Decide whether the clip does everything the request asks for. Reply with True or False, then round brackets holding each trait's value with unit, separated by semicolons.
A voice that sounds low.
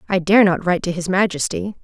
False (185 Hz)